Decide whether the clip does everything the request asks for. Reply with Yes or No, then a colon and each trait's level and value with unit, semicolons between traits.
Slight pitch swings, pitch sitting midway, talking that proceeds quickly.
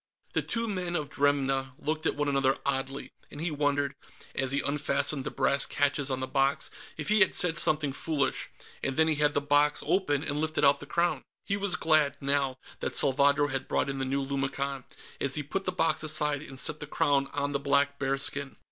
Yes: narrow, 1.9 semitones; medium, 145 Hz; fast, 210 wpm